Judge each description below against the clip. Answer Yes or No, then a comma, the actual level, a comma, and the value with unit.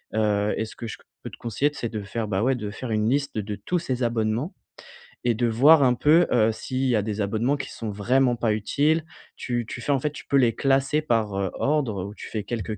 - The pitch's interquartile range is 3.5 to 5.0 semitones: Yes, average, 3.9 semitones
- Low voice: Yes, low, 120 Hz